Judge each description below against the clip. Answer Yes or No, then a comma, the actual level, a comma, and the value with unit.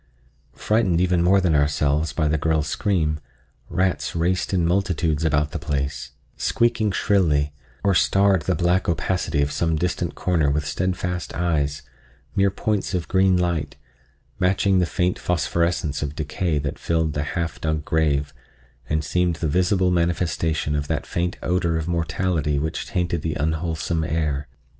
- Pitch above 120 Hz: No, very low, 85 Hz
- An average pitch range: Yes, average, 3.1 semitones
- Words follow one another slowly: No, average, 150 wpm